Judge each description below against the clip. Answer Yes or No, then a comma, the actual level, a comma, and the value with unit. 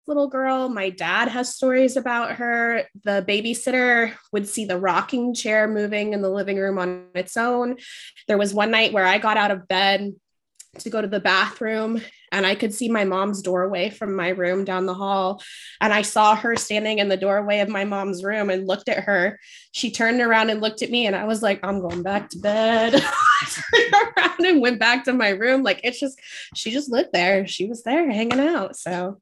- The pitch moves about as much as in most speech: Yes, average, 3.7 semitones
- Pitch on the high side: Yes, high, 215 Hz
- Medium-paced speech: No, fast, 215 wpm